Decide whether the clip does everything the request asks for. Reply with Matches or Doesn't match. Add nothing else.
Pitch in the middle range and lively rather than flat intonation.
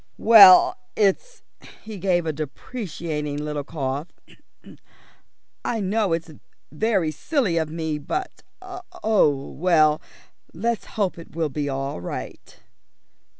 Matches